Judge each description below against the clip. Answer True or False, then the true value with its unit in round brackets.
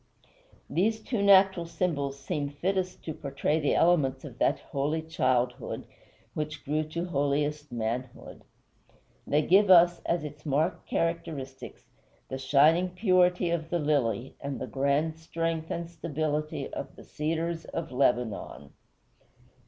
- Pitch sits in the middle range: True (155 Hz)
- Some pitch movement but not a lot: True (3.5 semitones)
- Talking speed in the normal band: False (130 wpm)